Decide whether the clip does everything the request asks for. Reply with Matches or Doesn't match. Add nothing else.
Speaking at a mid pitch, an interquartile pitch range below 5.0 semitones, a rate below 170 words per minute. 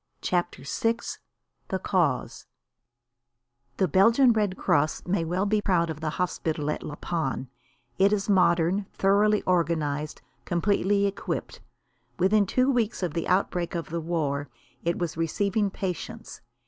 Matches